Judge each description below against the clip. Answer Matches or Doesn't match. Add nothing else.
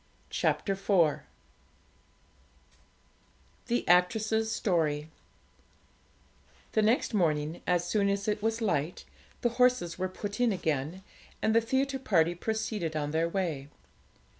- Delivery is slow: Matches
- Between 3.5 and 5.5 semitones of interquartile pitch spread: Matches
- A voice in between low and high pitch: Doesn't match